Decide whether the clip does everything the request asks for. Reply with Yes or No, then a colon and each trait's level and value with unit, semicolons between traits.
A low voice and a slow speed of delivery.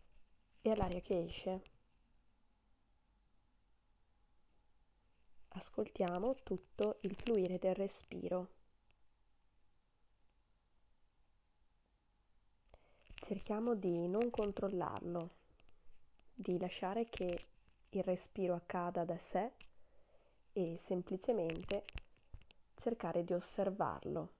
No: medium, 175 Hz; slow, 65 wpm